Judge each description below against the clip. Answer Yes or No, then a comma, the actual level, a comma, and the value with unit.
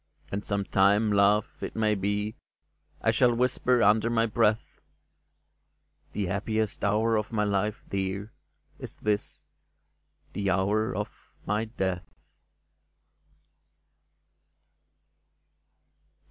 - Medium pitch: No, low, 105 Hz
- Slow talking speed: Yes, slow, 105 wpm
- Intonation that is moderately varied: No, narrow, 1.8 semitones